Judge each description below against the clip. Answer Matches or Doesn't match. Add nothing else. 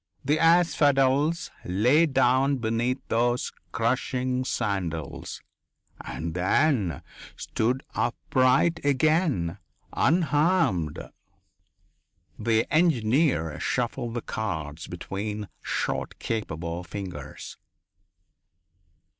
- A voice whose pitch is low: Matches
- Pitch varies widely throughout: Matches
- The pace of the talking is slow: Matches